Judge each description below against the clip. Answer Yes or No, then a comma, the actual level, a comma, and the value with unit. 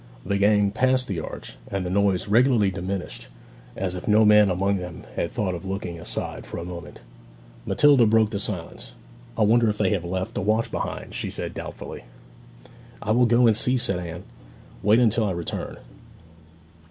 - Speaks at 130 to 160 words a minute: No, average, 180 wpm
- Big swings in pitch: No, average, 3.4 semitones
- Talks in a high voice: No, low, 100 Hz